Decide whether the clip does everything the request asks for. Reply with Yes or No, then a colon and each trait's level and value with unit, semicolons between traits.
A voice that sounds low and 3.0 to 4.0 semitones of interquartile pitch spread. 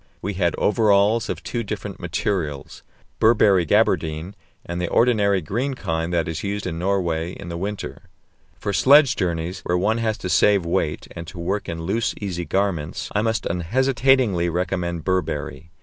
Yes: very low, 95 Hz; average, 3.7 semitones